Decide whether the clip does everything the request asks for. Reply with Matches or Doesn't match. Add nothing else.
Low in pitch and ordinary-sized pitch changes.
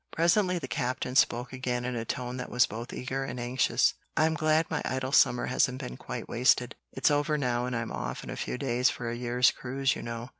Doesn't match